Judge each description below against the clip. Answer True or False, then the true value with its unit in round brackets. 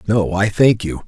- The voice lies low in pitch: True (100 Hz)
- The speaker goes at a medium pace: False (225 wpm)